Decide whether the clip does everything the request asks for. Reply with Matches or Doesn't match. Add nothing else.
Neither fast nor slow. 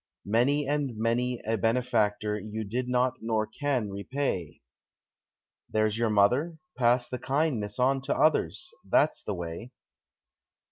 Doesn't match